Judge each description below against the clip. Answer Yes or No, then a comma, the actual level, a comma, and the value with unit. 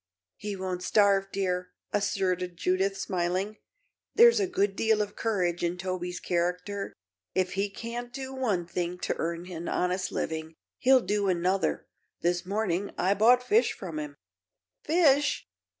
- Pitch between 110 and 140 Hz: No, high, 190 Hz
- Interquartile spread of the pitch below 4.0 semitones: Yes, average, 3.1 semitones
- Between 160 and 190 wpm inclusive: No, average, 145 wpm